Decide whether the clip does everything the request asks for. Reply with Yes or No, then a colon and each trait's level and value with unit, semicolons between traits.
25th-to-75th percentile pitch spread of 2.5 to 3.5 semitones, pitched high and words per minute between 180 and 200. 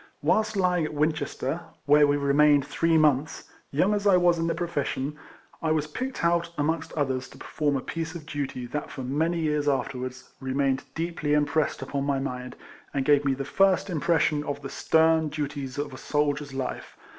No: average, 2.8 semitones; medium, 150 Hz; average, 190 wpm